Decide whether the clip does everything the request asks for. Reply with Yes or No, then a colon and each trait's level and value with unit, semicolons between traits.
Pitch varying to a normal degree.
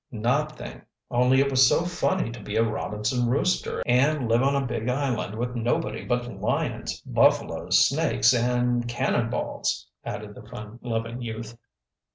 No: narrow, 2.3 semitones